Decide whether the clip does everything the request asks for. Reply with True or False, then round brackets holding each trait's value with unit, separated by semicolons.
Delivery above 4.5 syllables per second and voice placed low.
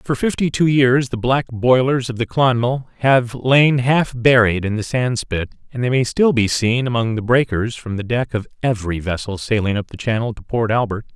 True (4.9 syllables/s; 120 Hz)